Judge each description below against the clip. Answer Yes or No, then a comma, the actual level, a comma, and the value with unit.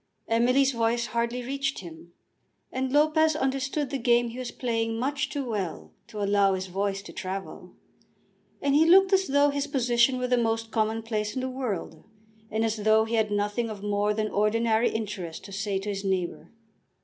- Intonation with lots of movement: No, average, 4.1 semitones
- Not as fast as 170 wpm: No, average, 185 wpm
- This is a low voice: No, high, 225 Hz